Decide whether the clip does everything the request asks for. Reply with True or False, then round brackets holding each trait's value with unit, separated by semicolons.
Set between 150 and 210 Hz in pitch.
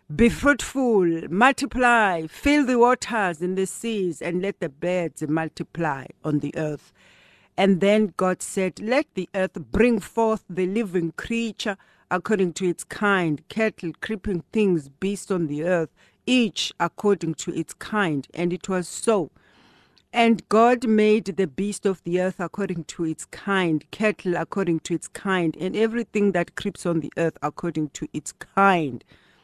True (185 Hz)